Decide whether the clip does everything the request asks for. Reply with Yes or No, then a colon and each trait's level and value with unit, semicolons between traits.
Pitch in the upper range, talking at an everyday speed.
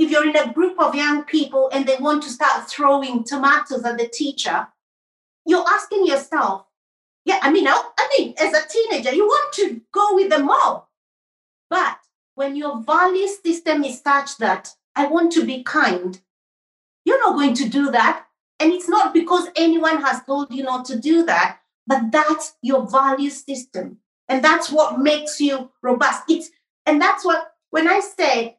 Yes: very high, 295 Hz; average, 185 wpm